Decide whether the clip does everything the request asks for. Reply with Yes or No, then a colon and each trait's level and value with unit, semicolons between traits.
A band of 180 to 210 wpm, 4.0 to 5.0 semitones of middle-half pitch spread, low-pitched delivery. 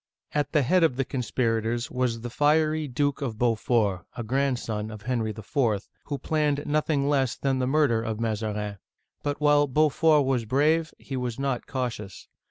Yes: average, 185 wpm; average, 4.3 semitones; low, 130 Hz